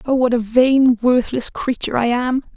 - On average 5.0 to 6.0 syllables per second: No, 4.7 syllables/s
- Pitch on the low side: No, high, 245 Hz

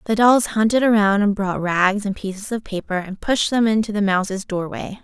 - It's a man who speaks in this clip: No, female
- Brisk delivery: Yes, fast, 215 wpm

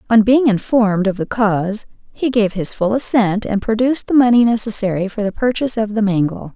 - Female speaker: Yes, female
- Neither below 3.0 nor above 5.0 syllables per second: No, 5.7 syllables/s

